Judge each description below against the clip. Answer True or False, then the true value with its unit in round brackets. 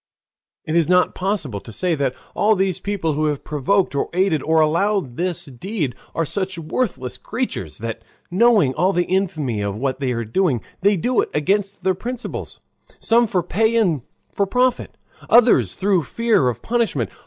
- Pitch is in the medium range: True (175 Hz)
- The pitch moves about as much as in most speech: False (6.3 semitones)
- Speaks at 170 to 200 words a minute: True (175 wpm)